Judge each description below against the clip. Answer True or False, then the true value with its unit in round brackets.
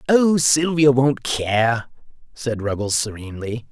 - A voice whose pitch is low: True (125 Hz)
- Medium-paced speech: False (115 wpm)